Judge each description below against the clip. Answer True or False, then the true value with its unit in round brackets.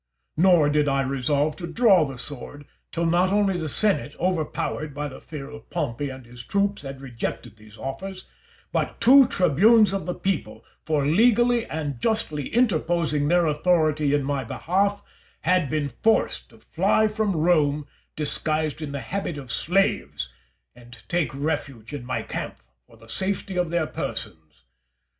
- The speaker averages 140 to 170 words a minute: True (160 wpm)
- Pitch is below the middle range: False (155 Hz)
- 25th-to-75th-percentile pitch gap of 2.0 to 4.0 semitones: False (5.1 semitones)